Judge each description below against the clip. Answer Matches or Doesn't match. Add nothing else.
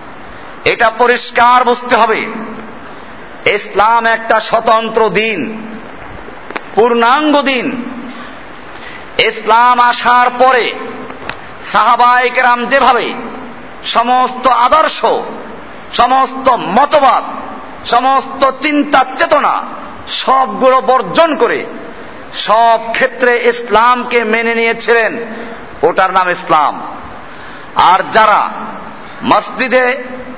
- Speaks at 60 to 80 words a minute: Matches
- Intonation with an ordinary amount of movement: Doesn't match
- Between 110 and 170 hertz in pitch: Doesn't match